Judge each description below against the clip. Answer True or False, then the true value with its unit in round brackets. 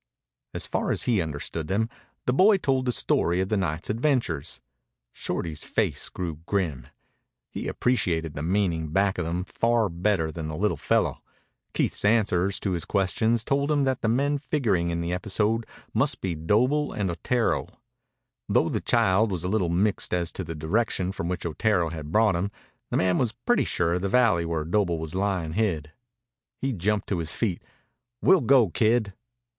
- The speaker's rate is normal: True (180 wpm)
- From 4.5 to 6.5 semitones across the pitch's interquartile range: True (5.0 semitones)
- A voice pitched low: True (95 Hz)